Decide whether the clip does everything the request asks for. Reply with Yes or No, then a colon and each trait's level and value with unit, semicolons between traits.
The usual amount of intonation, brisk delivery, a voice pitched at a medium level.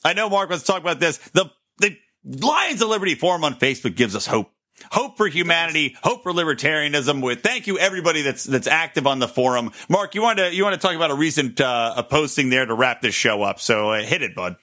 No: wide, 6.5 semitones; fast, 240 wpm; medium, 160 Hz